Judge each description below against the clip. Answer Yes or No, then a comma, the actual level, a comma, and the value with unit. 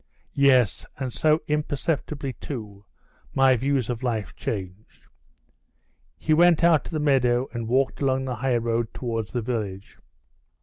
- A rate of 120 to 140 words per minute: Yes, slow, 135 wpm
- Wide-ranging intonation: No, average, 3.6 semitones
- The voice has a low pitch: Yes, low, 125 Hz